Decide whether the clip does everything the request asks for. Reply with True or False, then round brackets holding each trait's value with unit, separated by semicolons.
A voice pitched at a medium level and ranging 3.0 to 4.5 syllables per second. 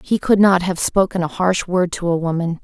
False (180 Hz; 5.1 syllables/s)